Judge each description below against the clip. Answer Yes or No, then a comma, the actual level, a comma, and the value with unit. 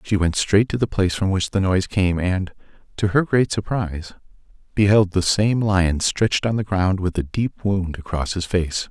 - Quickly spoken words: Yes, fast, 210 wpm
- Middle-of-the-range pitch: No, very low, 95 Hz